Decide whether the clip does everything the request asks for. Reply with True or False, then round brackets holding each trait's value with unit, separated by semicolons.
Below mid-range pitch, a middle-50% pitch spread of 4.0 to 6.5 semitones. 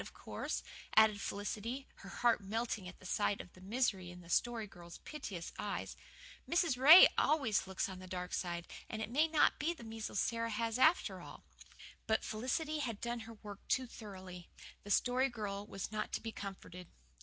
False (220 Hz; 4.3 semitones)